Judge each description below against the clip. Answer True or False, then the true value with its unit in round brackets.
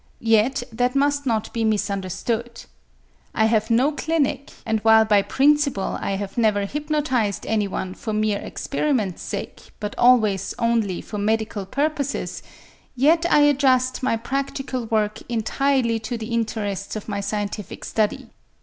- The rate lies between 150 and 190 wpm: False (140 wpm)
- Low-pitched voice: False (225 Hz)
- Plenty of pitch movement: False (4.2 semitones)